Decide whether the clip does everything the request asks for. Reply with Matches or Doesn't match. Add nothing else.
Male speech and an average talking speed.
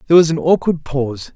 Doesn't match